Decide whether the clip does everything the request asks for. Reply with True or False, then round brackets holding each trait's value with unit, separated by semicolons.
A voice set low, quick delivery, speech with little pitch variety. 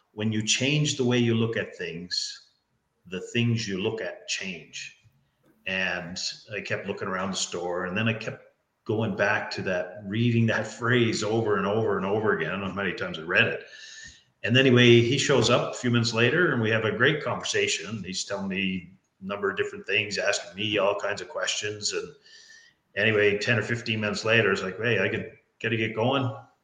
False (115 Hz; 215 wpm; 3.5 semitones)